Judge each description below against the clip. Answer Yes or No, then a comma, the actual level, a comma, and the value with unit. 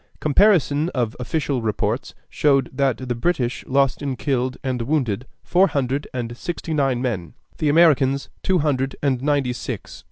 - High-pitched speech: No, low, 135 Hz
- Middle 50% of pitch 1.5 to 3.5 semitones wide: Yes, average, 3.0 semitones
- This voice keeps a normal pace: Yes, average, 155 wpm